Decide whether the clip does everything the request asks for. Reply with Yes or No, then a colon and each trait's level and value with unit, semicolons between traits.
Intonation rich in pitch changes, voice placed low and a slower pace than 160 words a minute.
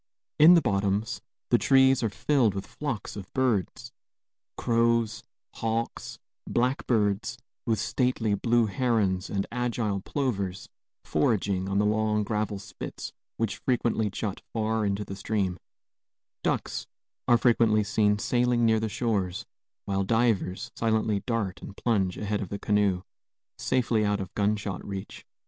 No: average, 2.8 semitones; low, 110 Hz; slow, 135 wpm